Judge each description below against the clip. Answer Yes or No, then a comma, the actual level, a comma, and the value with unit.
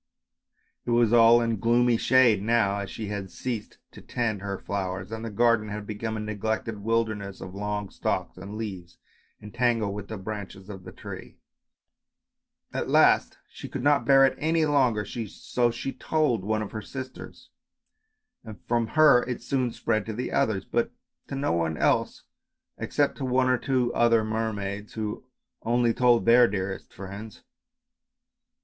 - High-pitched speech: No, low, 110 Hz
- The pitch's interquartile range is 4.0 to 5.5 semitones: No, average, 3.0 semitones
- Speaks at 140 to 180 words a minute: Yes, average, 165 wpm